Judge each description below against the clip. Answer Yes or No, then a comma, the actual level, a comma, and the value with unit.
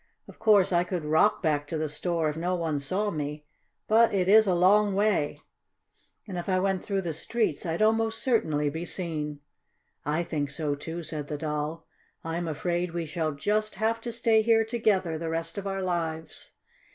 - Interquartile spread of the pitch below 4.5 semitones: No, average, 4.8 semitones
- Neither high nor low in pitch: Yes, medium, 175 Hz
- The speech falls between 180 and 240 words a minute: Yes, average, 190 wpm